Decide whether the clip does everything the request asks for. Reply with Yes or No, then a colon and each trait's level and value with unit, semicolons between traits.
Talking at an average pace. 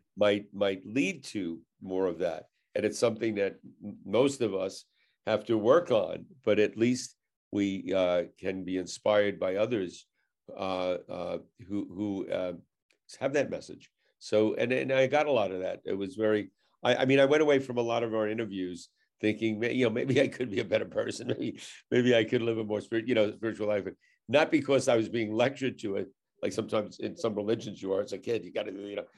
No: fast, 220 wpm